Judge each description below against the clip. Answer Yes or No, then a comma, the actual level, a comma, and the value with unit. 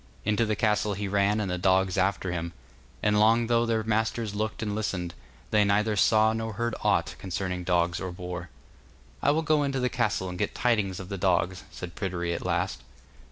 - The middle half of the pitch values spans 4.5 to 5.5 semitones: No, average, 3.3 semitones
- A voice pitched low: Yes, low, 100 Hz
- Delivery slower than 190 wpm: No, average, 200 wpm